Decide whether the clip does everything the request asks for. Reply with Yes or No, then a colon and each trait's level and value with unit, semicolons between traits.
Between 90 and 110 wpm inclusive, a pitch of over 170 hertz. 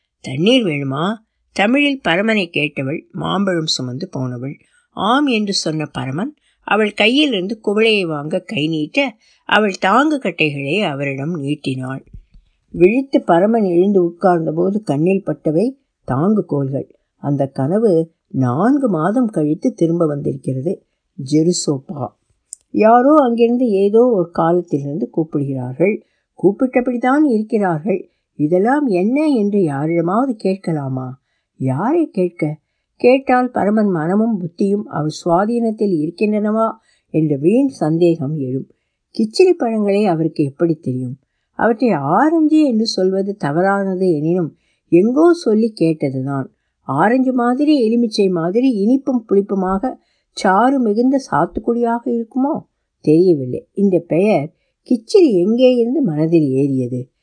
Yes: average, 100 wpm; high, 190 Hz